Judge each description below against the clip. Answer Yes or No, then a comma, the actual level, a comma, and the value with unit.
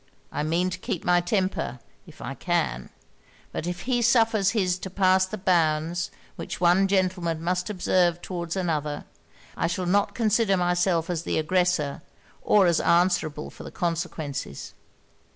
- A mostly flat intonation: Yes, narrow, 2.2 semitones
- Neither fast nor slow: Yes, average, 150 wpm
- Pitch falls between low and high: Yes, medium, 180 Hz